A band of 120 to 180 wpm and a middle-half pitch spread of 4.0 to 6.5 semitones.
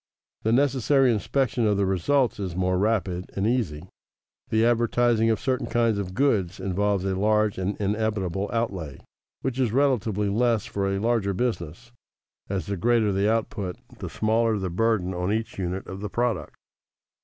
No: average, 165 wpm; average, 3.5 semitones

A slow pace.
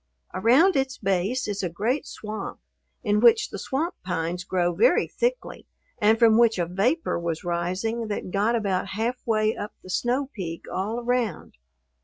No: average, 160 wpm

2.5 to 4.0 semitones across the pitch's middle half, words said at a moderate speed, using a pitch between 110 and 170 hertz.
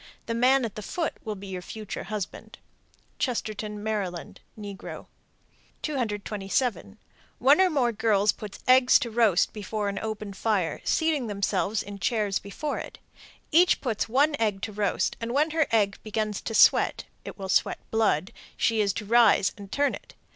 No: average, 3.2 semitones; average, 165 wpm; high, 215 Hz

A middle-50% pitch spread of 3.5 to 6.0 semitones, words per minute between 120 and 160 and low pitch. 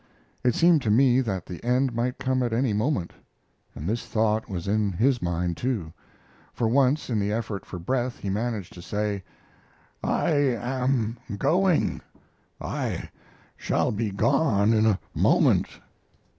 Yes: average, 4.1 semitones; average, 150 wpm; low, 115 Hz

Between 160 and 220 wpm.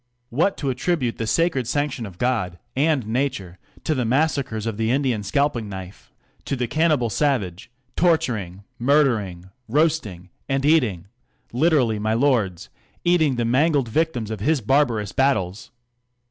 No: average, 145 wpm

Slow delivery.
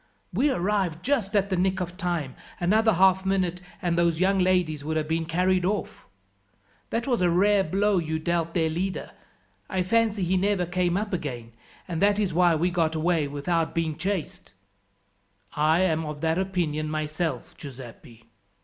No: average, 175 wpm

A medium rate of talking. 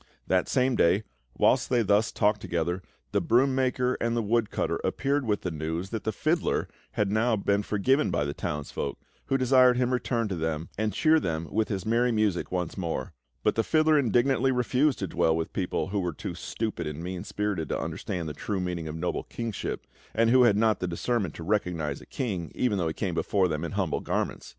No: fast, 210 wpm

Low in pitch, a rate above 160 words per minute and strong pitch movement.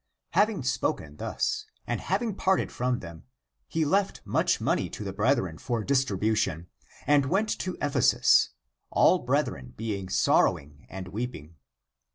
No: low, 115 Hz; average, 140 wpm; wide, 8.2 semitones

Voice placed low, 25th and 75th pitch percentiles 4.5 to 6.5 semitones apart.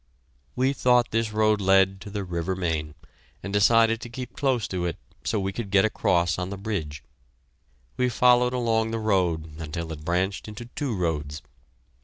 Yes: low, 100 Hz; average, 4.8 semitones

